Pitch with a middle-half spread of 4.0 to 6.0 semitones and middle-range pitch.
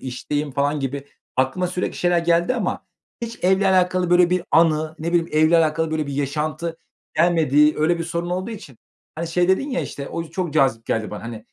No: average, 3.3 semitones; medium, 165 Hz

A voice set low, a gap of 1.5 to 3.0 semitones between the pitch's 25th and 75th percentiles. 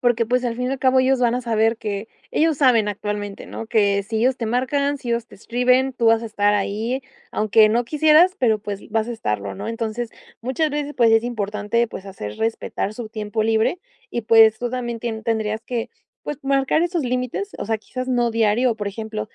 No: high, 230 Hz; average, 2.7 semitones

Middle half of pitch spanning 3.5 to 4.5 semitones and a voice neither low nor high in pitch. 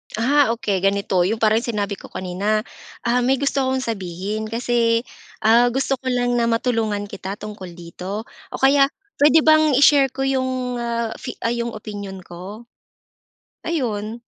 No: average, 4.0 semitones; high, 230 Hz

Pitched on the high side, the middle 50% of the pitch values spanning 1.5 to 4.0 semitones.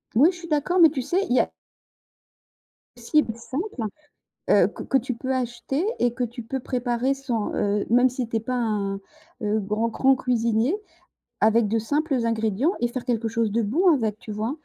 Yes: high, 240 Hz; average, 3.3 semitones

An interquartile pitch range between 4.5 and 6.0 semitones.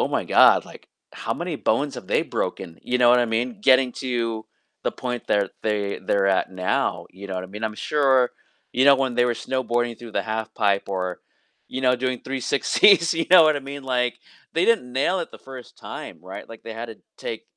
No: average, 3.3 semitones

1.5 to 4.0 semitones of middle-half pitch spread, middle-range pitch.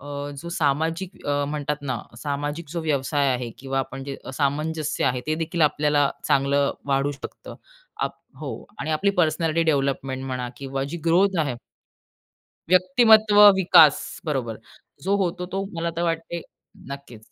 Yes: average, 3.6 semitones; medium, 150 Hz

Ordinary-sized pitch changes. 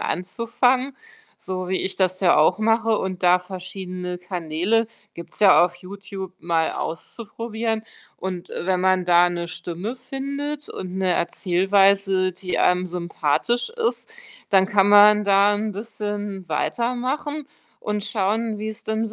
Yes: average, 3.6 semitones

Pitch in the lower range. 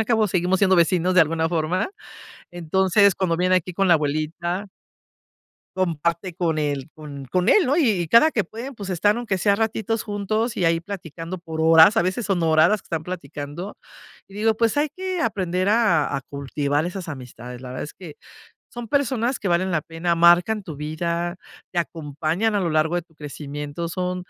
No: medium, 175 Hz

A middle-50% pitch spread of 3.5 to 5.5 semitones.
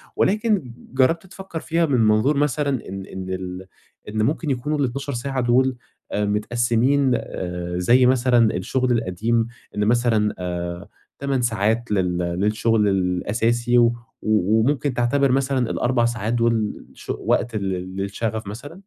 Yes: average, 4.1 semitones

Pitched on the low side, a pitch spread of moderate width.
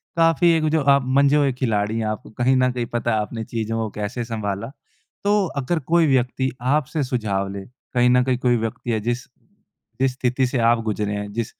Yes: low, 120 Hz; average, 3.2 semitones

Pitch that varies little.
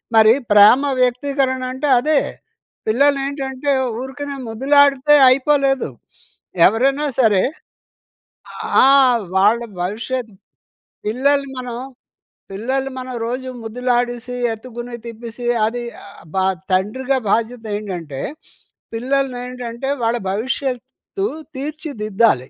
No: average, 3.3 semitones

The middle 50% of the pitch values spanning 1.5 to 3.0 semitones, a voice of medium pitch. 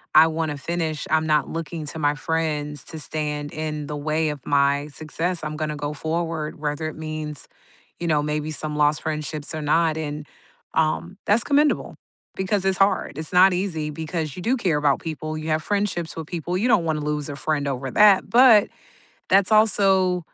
Yes: narrow, 2.6 semitones; medium, 155 Hz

